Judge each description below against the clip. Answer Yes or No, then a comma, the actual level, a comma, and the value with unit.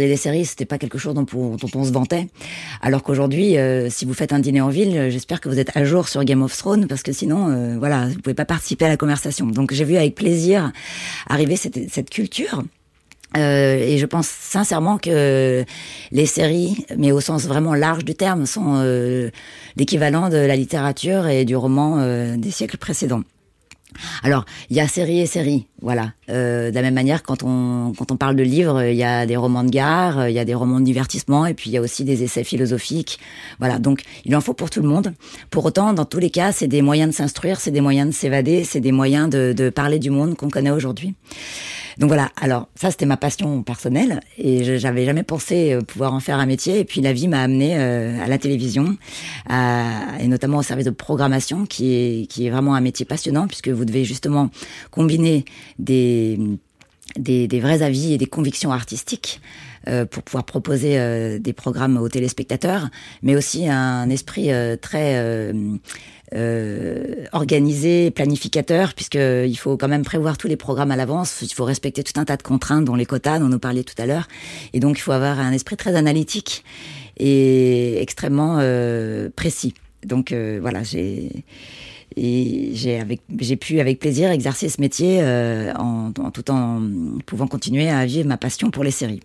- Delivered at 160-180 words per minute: No, average, 205 wpm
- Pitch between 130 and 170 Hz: Yes, low, 135 Hz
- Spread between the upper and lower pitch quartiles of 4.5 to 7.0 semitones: No, average, 3.3 semitones